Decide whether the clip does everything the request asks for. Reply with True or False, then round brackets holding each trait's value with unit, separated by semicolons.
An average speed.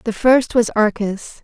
True (165 wpm)